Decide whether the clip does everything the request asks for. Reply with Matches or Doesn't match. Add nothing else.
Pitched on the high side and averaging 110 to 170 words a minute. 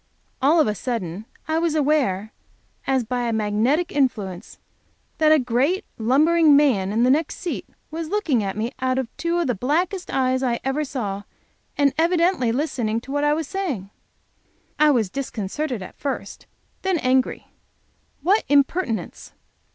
Matches